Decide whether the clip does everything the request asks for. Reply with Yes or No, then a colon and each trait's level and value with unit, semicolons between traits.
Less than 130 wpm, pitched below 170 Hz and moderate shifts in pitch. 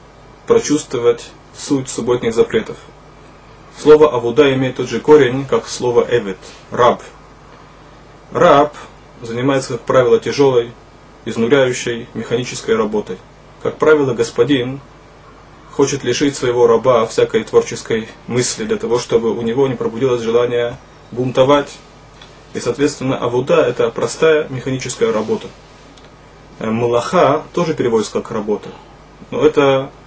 Yes: slow, 110 wpm; medium, 140 Hz; average, 3.8 semitones